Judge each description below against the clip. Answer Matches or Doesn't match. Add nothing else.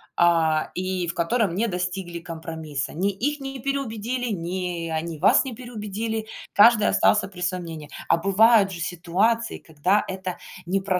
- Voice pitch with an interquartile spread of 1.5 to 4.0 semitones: Doesn't match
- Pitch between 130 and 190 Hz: Matches